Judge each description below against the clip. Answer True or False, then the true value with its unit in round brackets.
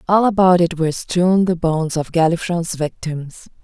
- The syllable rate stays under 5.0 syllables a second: True (4.8 syllables/s)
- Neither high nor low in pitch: True (170 Hz)